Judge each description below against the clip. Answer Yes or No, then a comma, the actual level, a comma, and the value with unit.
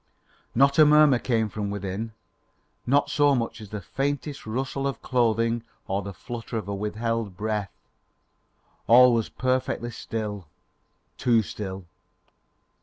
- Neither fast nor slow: No, slow, 130 wpm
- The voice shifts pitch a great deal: No, average, 3.6 semitones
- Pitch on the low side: Yes, low, 115 Hz